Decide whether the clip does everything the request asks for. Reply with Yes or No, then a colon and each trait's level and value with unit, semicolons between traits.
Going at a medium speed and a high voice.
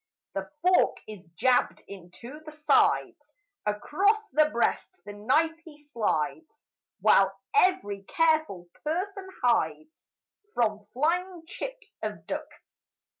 No: slow, 110 wpm; very high, 300 Hz